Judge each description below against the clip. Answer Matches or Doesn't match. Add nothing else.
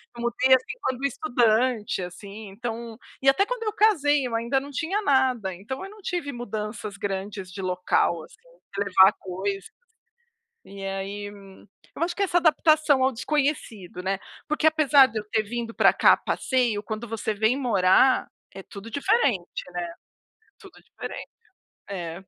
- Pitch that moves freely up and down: Matches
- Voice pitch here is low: Doesn't match